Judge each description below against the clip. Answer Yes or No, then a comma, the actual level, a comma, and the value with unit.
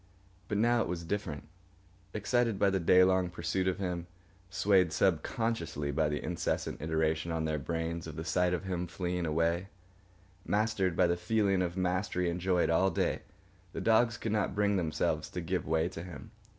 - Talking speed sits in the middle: Yes, average, 175 wpm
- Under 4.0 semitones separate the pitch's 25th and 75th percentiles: Yes, average, 2.9 semitones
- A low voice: Yes, very low, 90 Hz